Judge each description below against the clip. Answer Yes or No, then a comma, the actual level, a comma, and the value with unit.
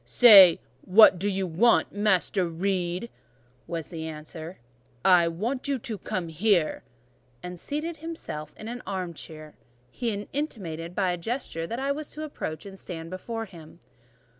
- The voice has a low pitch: No, medium, 185 Hz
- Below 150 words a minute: No, average, 155 wpm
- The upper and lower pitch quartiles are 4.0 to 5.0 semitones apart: No, wide, 5.6 semitones